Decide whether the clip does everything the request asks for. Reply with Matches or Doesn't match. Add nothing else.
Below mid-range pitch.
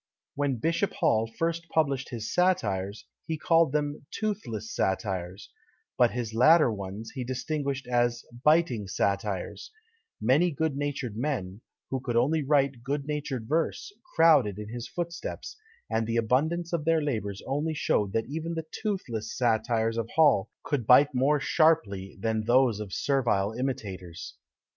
Matches